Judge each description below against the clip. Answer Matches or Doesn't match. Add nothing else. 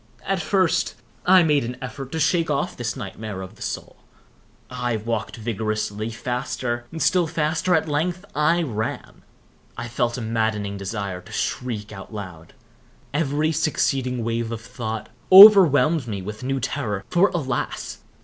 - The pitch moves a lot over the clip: Matches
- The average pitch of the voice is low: Matches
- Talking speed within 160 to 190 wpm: Doesn't match